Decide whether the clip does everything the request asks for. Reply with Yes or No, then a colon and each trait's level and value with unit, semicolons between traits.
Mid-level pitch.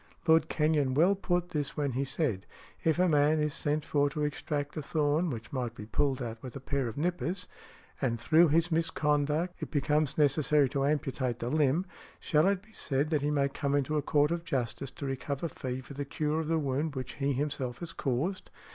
Yes: medium, 145 Hz